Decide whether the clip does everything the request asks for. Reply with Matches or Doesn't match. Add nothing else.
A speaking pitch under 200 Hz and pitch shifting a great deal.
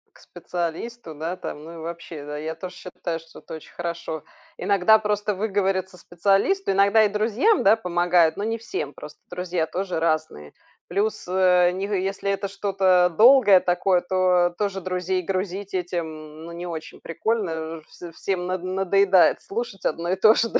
Doesn't match